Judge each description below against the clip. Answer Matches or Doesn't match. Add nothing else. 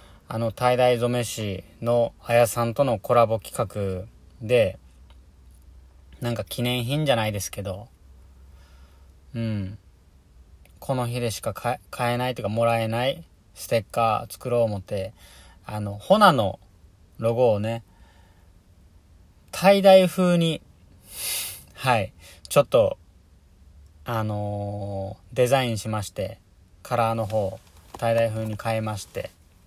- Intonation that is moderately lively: Doesn't match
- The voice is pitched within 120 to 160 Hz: Doesn't match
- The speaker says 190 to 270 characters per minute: Matches